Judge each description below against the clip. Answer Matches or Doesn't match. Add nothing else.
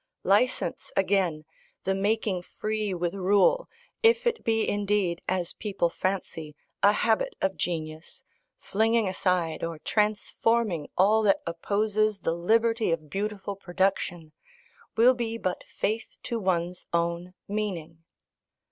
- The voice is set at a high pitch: Matches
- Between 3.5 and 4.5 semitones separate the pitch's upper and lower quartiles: Matches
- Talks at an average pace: Doesn't match